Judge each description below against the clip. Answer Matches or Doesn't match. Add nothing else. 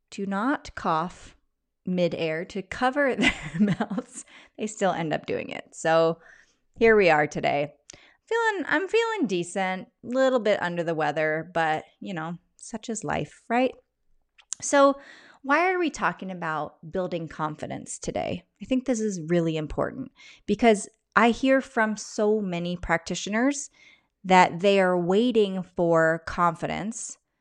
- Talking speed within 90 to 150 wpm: Matches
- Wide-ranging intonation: Matches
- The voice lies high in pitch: Matches